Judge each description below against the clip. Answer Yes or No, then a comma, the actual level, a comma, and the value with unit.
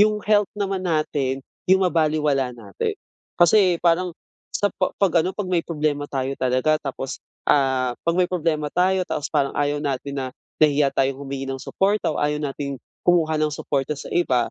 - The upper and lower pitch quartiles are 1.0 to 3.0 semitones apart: No, average, 4.4 semitones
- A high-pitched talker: No, medium, 150 Hz